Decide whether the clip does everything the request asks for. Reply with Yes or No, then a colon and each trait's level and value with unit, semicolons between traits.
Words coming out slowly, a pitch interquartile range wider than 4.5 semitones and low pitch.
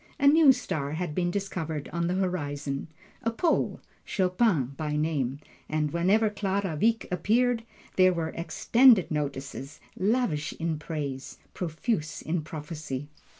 No: slow, 130 wpm; average, 5.1 semitones; medium, 170 Hz